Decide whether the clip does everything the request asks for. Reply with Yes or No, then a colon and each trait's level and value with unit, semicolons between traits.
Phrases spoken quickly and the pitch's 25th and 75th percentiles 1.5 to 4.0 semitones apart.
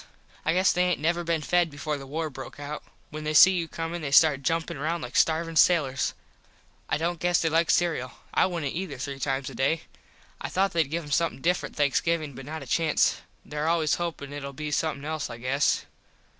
Yes: fast, 215 wpm; average, 3.0 semitones